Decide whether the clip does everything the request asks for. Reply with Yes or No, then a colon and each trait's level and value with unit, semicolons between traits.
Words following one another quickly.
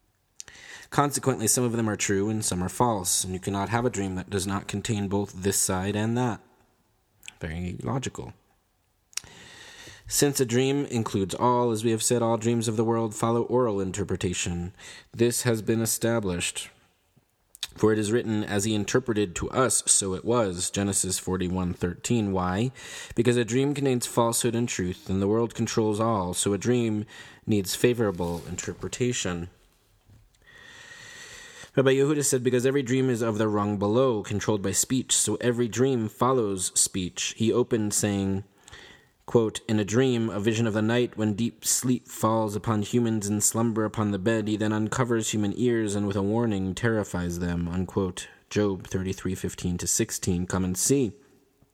No: average, 165 wpm